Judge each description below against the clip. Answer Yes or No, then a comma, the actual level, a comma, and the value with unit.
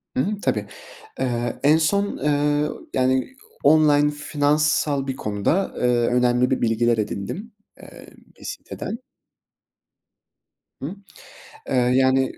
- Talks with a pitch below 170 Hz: Yes, low, 135 Hz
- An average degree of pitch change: Yes, average, 3.5 semitones